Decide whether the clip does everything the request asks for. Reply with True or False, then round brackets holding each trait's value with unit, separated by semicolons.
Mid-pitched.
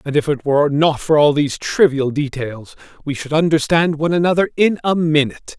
True (150 Hz)